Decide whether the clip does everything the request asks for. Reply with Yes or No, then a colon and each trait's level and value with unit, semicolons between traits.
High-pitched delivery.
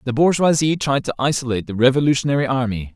No: low, 135 Hz